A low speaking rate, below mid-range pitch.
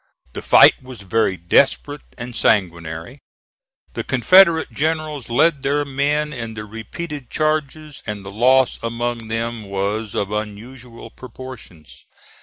Yes: slow, 125 wpm; low, 120 Hz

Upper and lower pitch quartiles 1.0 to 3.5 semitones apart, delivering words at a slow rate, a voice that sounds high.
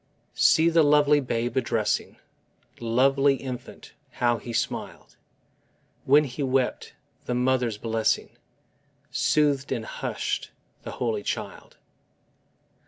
No: average, 3.1 semitones; slow, 105 wpm; low, 130 Hz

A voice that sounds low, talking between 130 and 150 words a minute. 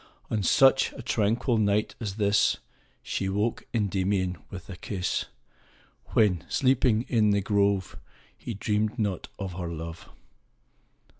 Yes: low, 100 Hz; slow, 135 wpm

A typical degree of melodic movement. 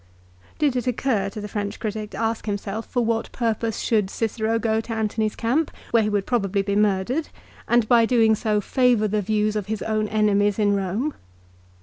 No: narrow, 1.8 semitones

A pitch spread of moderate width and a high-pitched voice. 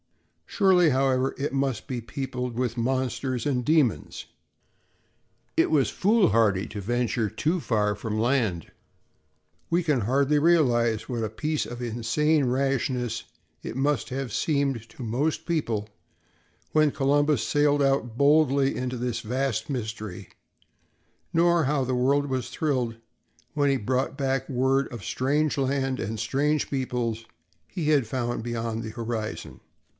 No: average, 3.6 semitones; low, 130 Hz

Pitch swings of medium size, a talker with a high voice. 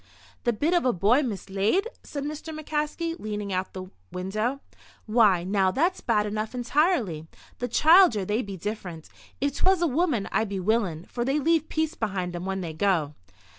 No: wide, 7.6 semitones; high, 220 Hz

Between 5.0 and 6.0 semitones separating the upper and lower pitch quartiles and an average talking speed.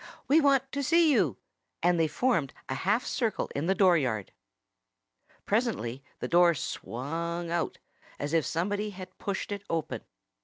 Yes: wide, 5.5 semitones; average, 150 wpm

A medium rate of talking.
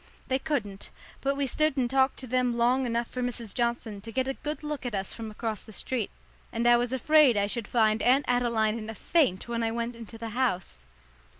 No: fast, 225 wpm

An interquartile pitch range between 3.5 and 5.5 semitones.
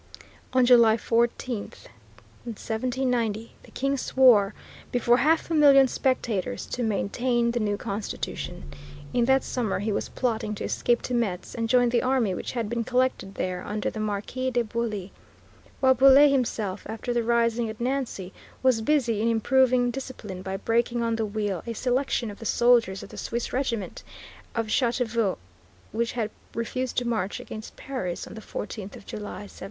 No: average, 3.1 semitones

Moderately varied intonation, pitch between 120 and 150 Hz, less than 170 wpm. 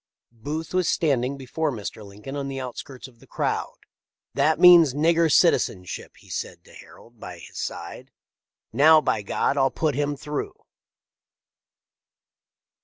Yes: average, 4.5 semitones; medium, 140 Hz; average, 150 wpm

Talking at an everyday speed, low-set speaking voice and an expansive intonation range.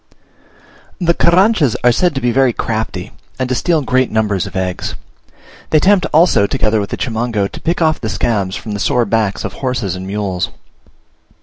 Yes: average, 185 wpm; low, 120 Hz; wide, 6.3 semitones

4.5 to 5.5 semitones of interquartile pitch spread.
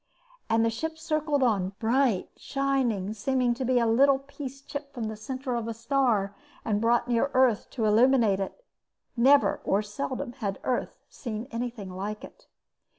No: average, 3.9 semitones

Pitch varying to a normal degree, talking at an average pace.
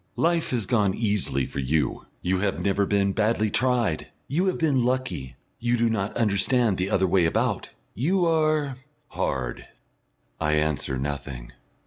No: wide, 7.2 semitones; average, 150 wpm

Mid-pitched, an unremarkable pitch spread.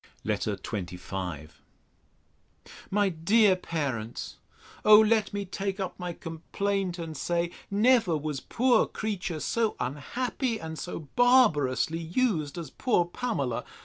No: medium, 175 Hz; wide, 5.8 semitones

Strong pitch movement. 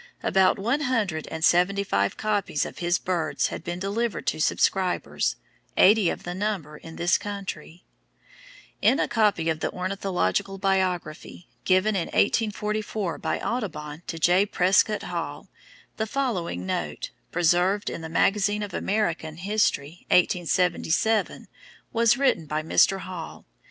No: average, 3.9 semitones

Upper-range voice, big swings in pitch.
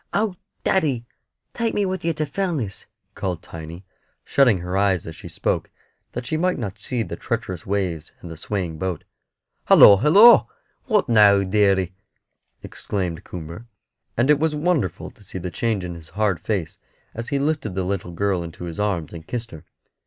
No: low, 100 Hz; wide, 7.8 semitones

